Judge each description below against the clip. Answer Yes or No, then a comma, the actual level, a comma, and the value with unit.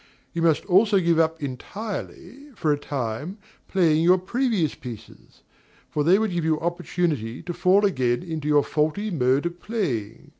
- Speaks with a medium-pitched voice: Yes, medium, 165 Hz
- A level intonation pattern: No, average, 4.4 semitones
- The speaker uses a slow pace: No, average, 160 wpm